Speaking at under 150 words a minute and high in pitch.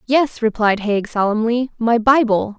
Yes: average, 140 wpm; high, 230 Hz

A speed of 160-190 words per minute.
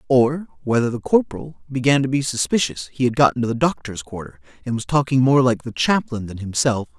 No: fast, 205 wpm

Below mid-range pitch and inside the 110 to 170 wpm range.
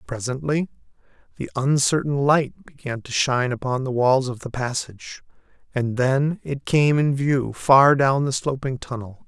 Yes: low, 130 Hz; average, 155 wpm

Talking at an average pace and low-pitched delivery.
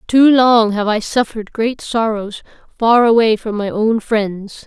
No: average, 165 wpm; high, 225 Hz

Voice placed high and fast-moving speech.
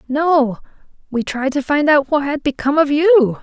No: very high, 285 Hz; average, 195 wpm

